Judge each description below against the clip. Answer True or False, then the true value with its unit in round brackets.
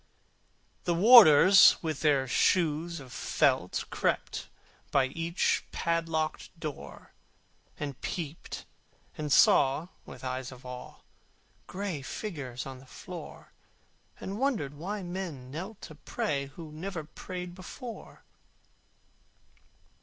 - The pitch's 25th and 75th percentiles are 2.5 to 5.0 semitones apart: True (4.7 semitones)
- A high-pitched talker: False (160 Hz)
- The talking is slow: True (110 wpm)